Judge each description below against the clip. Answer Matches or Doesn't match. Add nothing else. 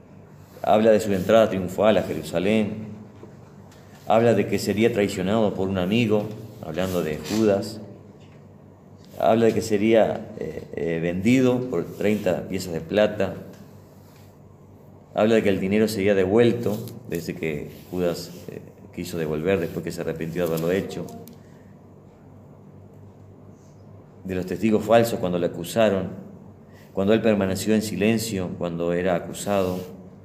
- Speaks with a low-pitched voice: Matches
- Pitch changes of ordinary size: Matches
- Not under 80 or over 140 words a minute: Matches